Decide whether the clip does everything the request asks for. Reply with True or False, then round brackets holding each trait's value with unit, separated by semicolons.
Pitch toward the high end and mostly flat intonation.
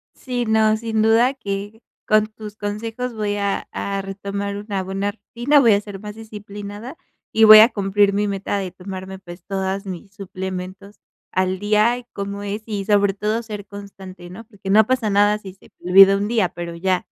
True (205 Hz; 1.9 semitones)